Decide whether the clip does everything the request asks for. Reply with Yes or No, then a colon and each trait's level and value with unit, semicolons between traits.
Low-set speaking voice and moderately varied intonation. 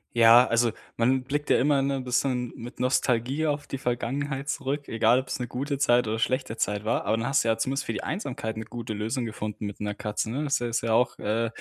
Yes: low, 120 Hz; average, 3.2 semitones